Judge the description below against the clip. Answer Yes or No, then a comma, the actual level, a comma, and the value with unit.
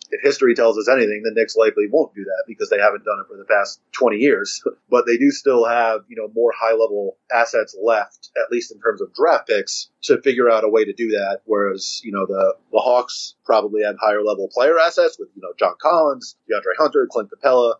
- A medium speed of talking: No, fast, 235 wpm